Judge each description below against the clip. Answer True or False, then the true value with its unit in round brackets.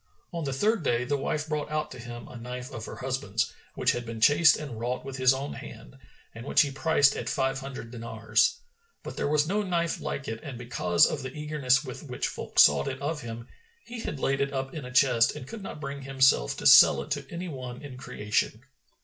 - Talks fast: True (230 wpm)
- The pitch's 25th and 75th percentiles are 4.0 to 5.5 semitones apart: False (3.5 semitones)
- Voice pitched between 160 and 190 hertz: False (135 Hz)